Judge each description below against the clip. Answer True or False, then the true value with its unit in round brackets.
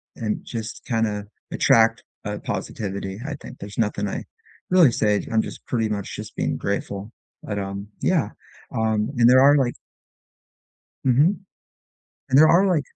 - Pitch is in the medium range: False (110 Hz)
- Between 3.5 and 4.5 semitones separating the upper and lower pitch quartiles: True (4.1 semitones)